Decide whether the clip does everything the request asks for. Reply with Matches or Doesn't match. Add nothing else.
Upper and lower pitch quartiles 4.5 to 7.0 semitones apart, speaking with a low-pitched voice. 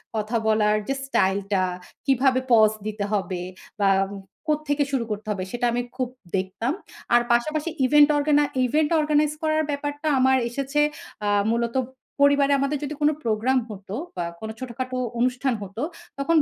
Doesn't match